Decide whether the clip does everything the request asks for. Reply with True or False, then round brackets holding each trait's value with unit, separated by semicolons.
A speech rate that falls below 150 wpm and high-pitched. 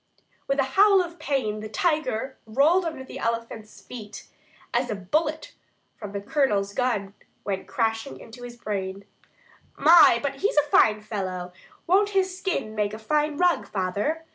False (160 wpm; 245 Hz)